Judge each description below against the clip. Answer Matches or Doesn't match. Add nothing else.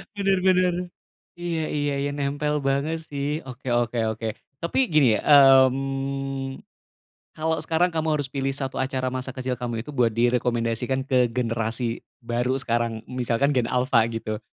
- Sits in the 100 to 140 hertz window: Matches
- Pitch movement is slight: Doesn't match